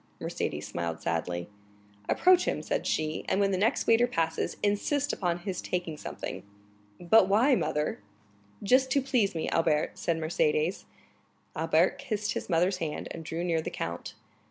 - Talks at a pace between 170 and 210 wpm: No, average, 155 wpm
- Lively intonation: Yes, wide, 6.0 semitones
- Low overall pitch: No, medium, 180 Hz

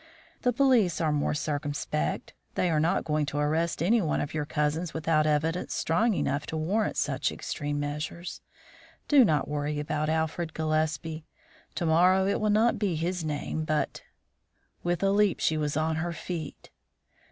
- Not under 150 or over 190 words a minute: Yes, average, 170 wpm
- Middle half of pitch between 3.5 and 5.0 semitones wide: No, average, 2.8 semitones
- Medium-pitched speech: Yes, medium, 160 Hz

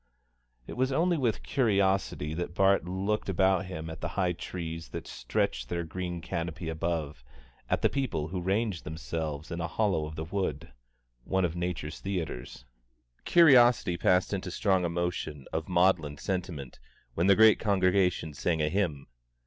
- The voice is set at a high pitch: No, very low, 90 Hz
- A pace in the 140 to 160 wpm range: Yes, average, 155 wpm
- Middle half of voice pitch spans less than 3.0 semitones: No, average, 3.3 semitones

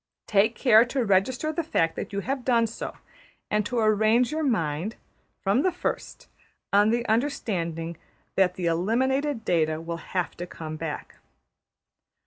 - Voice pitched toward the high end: Yes, high, 215 Hz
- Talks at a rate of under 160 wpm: Yes, average, 150 wpm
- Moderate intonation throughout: No, wide, 6.4 semitones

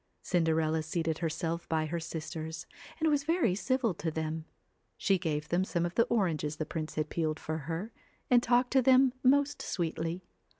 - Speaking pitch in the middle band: Yes, medium, 170 Hz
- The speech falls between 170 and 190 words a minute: Yes, average, 185 wpm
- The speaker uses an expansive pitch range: Yes, wide, 6.7 semitones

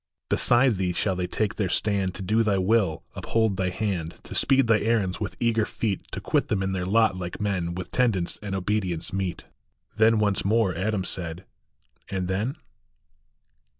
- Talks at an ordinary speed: Yes, average, 185 wpm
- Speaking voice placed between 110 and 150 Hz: No, low, 100 Hz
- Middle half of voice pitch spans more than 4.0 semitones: No, average, 3.2 semitones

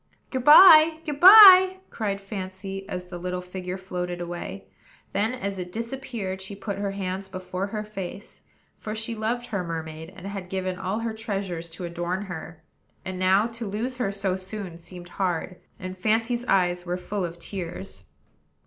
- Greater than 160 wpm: Yes, average, 170 wpm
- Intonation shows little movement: No, average, 3.3 semitones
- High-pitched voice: Yes, high, 195 Hz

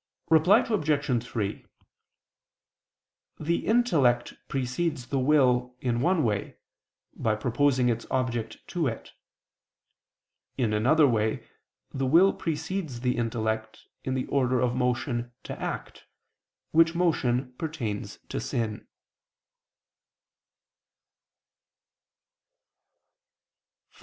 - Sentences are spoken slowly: Yes, slow, 90 wpm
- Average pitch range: Yes, average, 4.6 semitones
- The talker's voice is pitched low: Yes, low, 125 Hz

